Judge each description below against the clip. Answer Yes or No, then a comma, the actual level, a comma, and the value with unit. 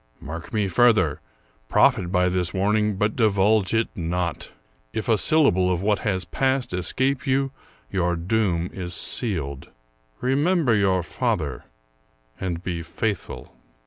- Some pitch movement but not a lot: Yes, average, 4.3 semitones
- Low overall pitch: Yes, very low, 95 Hz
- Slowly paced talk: Yes, slow, 130 wpm